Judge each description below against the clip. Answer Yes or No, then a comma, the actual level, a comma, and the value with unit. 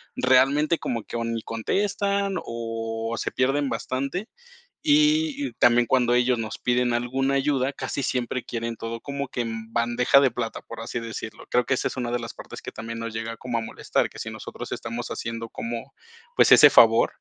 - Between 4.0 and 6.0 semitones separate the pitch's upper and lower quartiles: No, average, 2.8 semitones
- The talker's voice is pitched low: Yes, low, 120 Hz